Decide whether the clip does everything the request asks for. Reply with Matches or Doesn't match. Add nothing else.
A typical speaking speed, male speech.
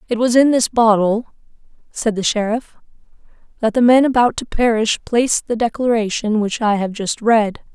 Doesn't match